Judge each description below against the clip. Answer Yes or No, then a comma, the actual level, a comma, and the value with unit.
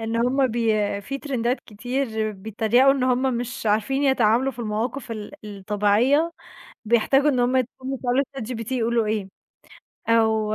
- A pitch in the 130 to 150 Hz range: No, high, 235 Hz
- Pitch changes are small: No, average, 3.2 semitones